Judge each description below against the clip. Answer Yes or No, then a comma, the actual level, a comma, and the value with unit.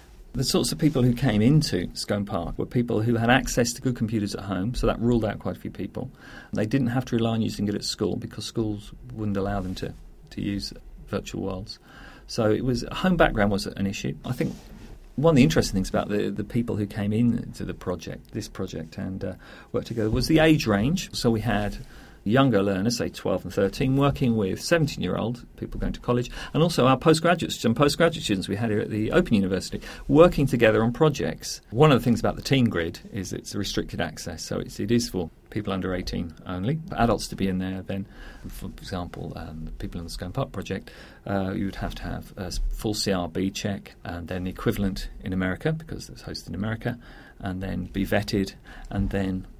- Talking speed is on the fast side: Yes, fast, 220 wpm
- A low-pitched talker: Yes, low, 110 Hz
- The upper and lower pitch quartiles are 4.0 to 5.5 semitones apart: Yes, average, 4.3 semitones